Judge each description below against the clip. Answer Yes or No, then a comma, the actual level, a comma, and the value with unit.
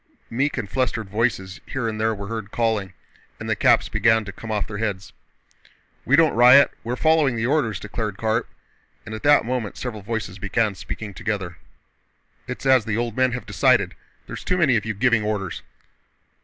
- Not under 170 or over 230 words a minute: Yes, average, 180 wpm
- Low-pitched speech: Yes, low, 110 Hz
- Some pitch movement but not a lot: Yes, average, 3.1 semitones